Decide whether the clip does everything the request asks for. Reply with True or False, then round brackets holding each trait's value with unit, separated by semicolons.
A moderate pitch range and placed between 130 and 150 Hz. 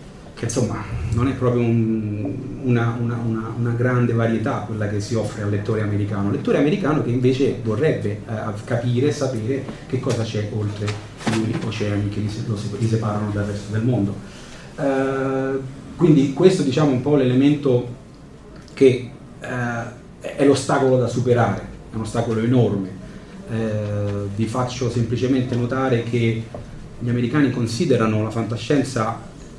False (3.1 semitones; 120 Hz)